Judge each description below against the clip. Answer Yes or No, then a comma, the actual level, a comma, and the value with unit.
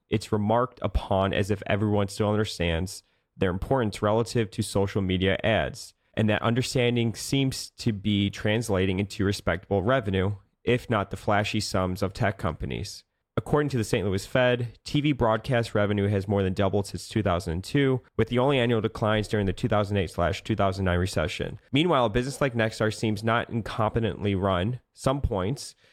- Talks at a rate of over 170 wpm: No, average, 160 wpm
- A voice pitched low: Yes, low, 105 Hz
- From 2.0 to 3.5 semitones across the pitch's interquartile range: Yes, average, 3.1 semitones